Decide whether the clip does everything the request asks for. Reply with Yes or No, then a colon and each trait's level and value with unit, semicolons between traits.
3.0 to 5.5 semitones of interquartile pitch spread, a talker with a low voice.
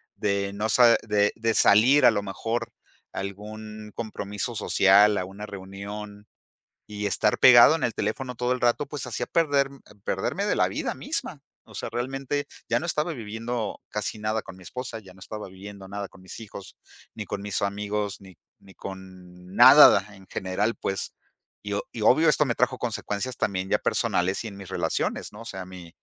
Yes: average, 3.3 semitones; low, 105 Hz